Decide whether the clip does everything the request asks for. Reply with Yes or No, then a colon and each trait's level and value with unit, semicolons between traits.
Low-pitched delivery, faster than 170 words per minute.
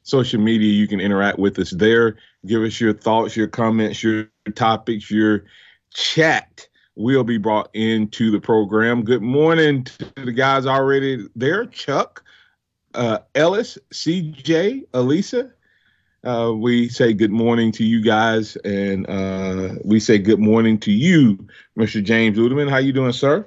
No: low, 115 Hz; average, 150 wpm